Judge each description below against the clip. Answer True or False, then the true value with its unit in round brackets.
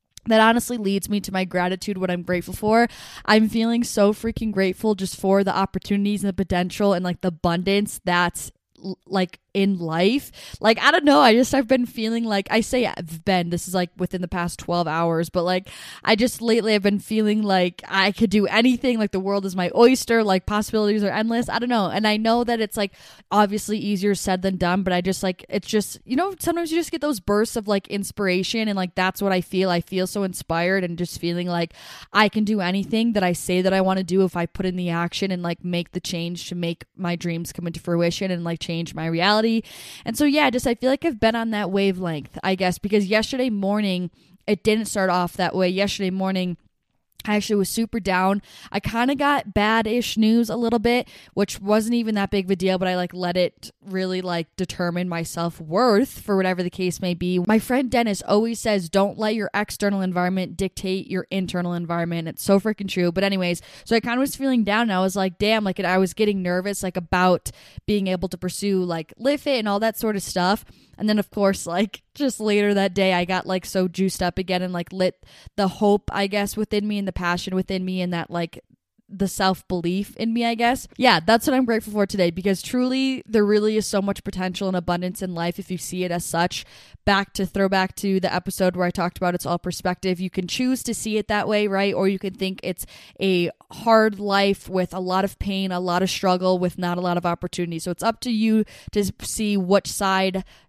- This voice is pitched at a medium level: False (195 Hz)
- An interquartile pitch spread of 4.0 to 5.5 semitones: False (2.9 semitones)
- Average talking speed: False (235 wpm)